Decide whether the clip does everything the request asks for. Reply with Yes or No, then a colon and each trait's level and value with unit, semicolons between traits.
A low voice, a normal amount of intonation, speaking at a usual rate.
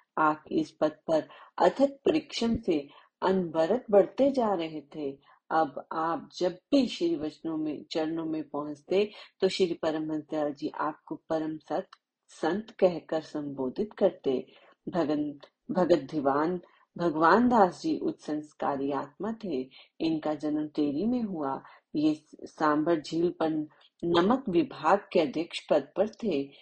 No: medium, 165 Hz; average, 5.0 semitones; average, 130 wpm